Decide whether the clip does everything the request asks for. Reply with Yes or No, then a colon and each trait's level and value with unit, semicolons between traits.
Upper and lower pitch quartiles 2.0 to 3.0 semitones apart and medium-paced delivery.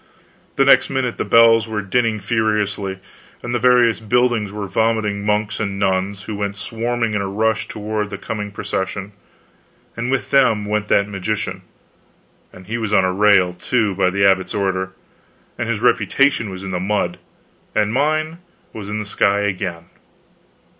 Yes: narrow, 2.5 semitones; average, 165 wpm